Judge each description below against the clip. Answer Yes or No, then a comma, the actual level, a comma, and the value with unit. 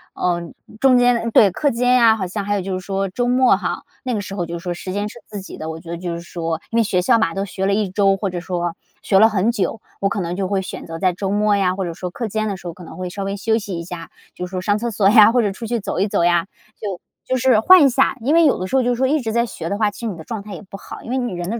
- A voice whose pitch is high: Yes, high, 200 Hz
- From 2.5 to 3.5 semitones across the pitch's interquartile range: No, average, 4.1 semitones